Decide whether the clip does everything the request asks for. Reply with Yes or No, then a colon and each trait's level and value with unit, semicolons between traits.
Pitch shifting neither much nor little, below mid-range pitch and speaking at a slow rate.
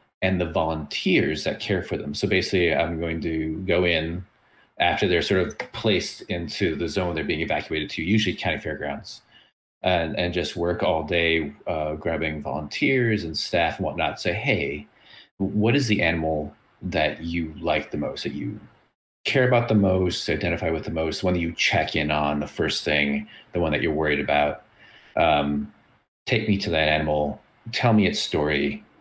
No: average, 4.3 semitones; very low, 85 Hz; average, 180 wpm